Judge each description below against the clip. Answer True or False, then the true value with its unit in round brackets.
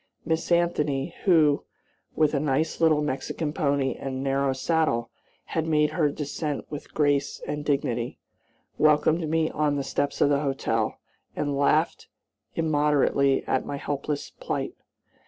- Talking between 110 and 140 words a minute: True (135 wpm)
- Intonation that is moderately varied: False (2.0 semitones)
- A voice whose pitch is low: False (145 Hz)